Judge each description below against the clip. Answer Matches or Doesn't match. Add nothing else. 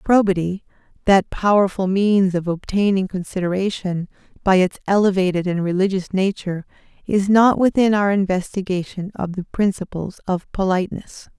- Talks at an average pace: Doesn't match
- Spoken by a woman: Matches